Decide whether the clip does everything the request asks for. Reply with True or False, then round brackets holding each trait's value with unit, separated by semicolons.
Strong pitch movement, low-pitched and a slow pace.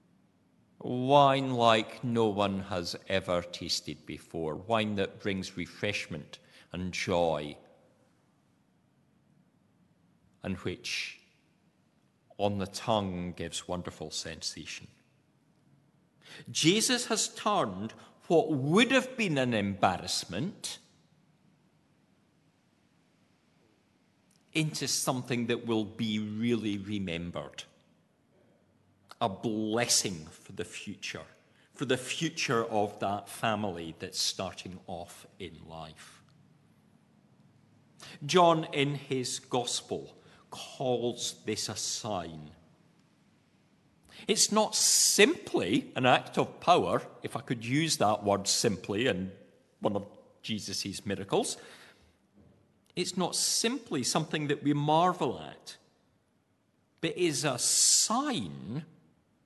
True (7.0 semitones; 115 Hz; 95 wpm)